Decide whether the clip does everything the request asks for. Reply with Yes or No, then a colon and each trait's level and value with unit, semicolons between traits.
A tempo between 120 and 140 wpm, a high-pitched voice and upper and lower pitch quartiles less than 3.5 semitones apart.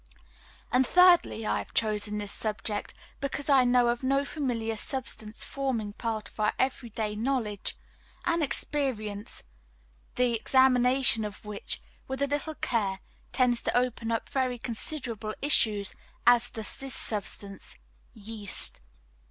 No: slow, 135 wpm; high, 235 Hz; average, 3.8 semitones